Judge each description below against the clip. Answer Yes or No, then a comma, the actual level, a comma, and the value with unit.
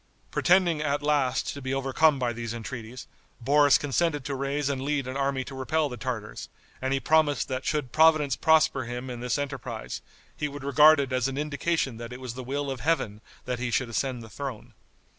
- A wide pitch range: No, average, 2.7 semitones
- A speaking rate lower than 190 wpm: No, fast, 205 wpm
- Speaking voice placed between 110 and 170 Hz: Yes, low, 135 Hz